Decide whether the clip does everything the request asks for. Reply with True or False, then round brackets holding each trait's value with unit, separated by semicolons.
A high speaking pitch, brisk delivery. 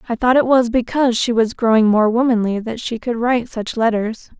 True (235 Hz; 220 wpm)